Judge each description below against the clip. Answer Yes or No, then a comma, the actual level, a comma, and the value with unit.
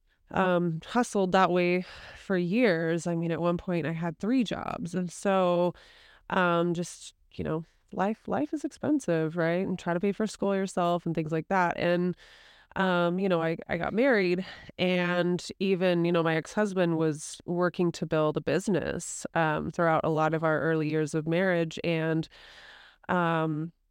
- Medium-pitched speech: Yes, medium, 175 Hz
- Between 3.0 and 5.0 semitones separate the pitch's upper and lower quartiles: No, narrow, 2.4 semitones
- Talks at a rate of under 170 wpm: No, average, 175 wpm